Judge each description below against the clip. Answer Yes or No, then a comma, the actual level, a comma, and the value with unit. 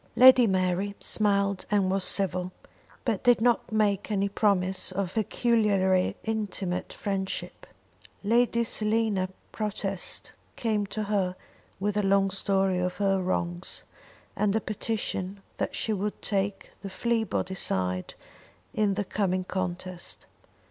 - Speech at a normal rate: No, slow, 125 wpm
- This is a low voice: No, high, 200 Hz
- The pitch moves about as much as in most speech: No, narrow, 2.2 semitones